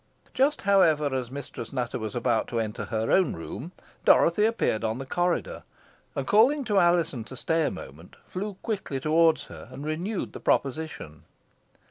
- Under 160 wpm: No, average, 165 wpm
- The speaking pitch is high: No, medium, 155 Hz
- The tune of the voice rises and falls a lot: Yes, wide, 7.4 semitones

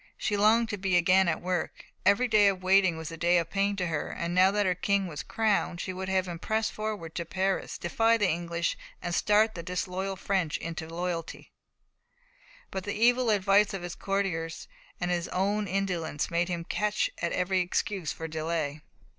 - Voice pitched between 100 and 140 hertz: No, medium, 185 Hz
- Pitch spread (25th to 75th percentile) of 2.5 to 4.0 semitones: Yes, average, 2.9 semitones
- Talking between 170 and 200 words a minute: Yes, average, 190 wpm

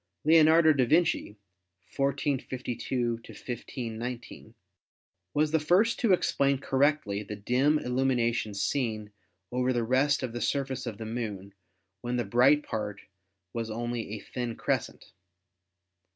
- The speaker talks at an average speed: No, slow, 125 wpm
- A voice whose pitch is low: Yes, low, 125 Hz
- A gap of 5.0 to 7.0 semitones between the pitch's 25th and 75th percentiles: No, average, 3.6 semitones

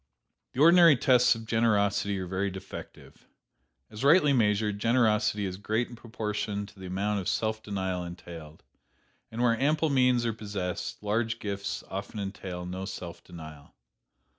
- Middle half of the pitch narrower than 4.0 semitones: Yes, average, 3.3 semitones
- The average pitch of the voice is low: Yes, low, 105 Hz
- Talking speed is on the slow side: No, average, 150 wpm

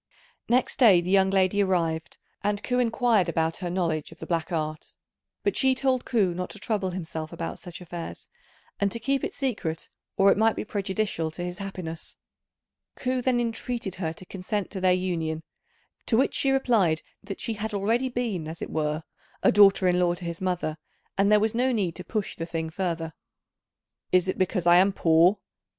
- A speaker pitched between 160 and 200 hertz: Yes, high, 190 Hz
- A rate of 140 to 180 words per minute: No, average, 195 wpm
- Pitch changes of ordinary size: Yes, average, 4.5 semitones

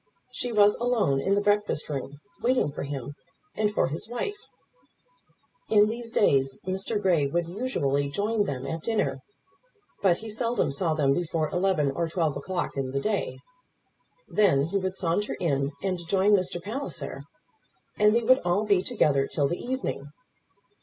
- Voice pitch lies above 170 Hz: Yes, medium, 185 Hz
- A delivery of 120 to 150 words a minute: No, average, 160 wpm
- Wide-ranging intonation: Yes, wide, 6.6 semitones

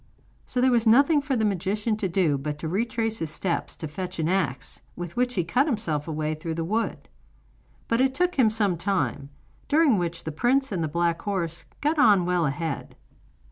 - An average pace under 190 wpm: No, fast, 205 wpm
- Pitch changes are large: Yes, wide, 6.1 semitones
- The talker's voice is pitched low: No, high, 190 Hz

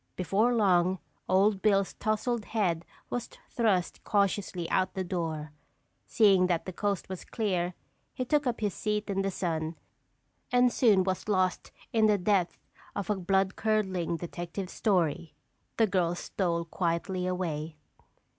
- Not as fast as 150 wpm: Yes, average, 140 wpm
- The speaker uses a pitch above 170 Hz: Yes, high, 190 Hz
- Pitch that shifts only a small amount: No, average, 3.2 semitones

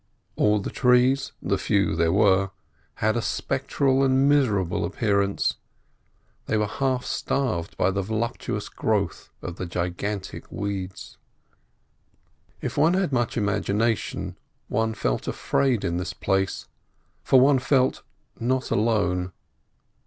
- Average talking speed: No, slow, 115 wpm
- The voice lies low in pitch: Yes, low, 105 Hz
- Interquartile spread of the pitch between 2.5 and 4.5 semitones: No, average, 5.1 semitones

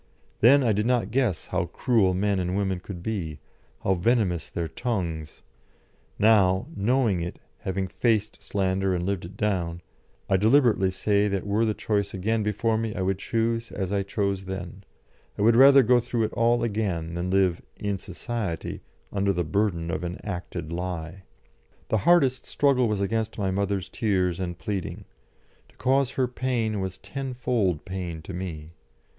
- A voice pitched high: No, low, 100 Hz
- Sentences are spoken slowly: No, average, 165 wpm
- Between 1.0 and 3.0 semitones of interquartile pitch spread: No, average, 3.7 semitones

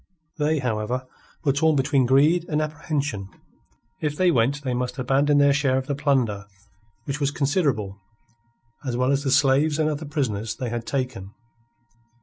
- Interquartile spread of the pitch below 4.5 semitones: Yes, average, 2.9 semitones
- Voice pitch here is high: No, medium, 140 Hz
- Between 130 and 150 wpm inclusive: No, average, 160 wpm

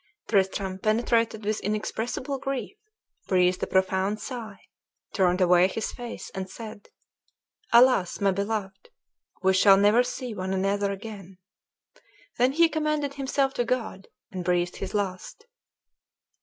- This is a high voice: Yes, high, 210 Hz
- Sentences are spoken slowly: Yes, slow, 130 wpm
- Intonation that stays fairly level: No, average, 4.3 semitones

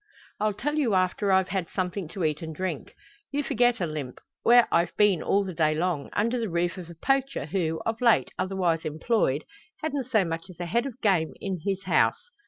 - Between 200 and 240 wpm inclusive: Yes, fast, 205 wpm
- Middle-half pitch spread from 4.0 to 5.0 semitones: No, wide, 5.4 semitones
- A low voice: No, high, 190 Hz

